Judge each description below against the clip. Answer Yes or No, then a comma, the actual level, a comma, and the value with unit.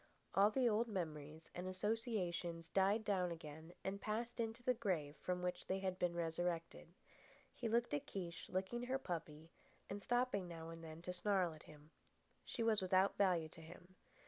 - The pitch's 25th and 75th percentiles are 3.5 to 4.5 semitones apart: Yes, average, 4.2 semitones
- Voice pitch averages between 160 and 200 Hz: Yes, medium, 185 Hz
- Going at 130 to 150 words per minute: No, average, 175 wpm